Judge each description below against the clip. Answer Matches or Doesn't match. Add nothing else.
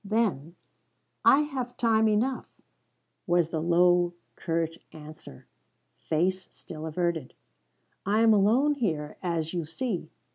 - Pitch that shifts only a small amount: Doesn't match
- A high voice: Doesn't match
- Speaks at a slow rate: Matches